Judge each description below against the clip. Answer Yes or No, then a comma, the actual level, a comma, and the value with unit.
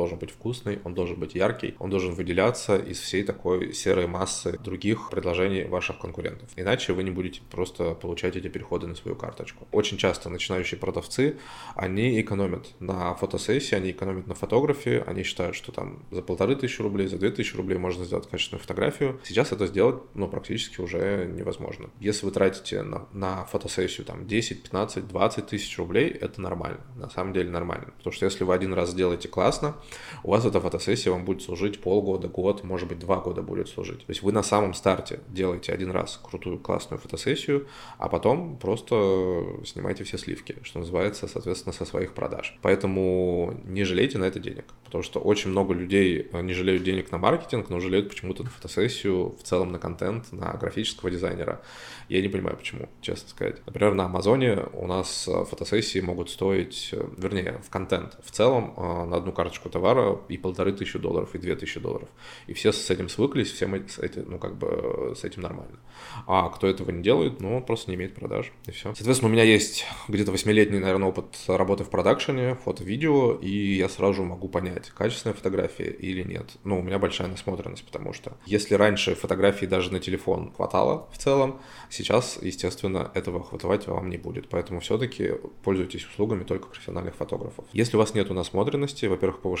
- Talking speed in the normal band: No, fast, 185 wpm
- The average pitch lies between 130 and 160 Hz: No, very low, 95 Hz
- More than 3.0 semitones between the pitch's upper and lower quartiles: No, average, 2.7 semitones